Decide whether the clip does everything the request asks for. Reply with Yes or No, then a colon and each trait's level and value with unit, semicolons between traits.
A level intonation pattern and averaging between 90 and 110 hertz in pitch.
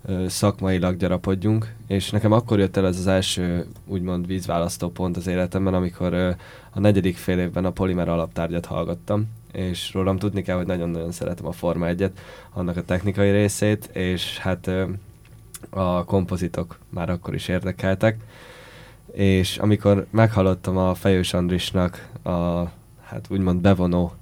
Yes: narrow, 2.0 semitones; very low, 95 Hz